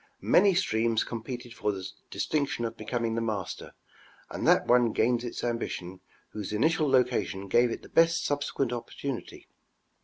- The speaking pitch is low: Yes, low, 120 Hz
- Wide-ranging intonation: No, average, 3.3 semitones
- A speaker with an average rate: Yes, average, 150 wpm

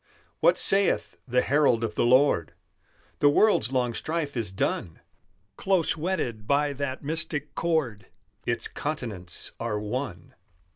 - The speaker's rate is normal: No, slow, 130 wpm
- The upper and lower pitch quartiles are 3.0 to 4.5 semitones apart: No, wide, 5.5 semitones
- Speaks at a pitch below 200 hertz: Yes, low, 135 Hz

